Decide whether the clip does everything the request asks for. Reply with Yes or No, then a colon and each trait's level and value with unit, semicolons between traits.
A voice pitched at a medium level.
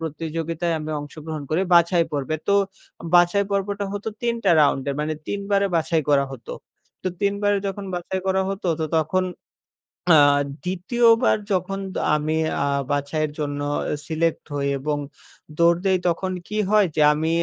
Yes: medium, 170 Hz